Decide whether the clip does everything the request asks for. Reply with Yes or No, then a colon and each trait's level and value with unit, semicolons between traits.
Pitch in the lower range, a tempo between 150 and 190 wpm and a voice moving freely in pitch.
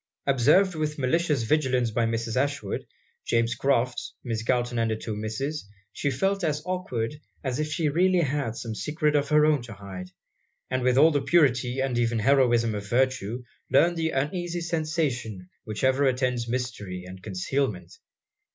No: low, 130 Hz; average, 165 wpm; average, 4.6 semitones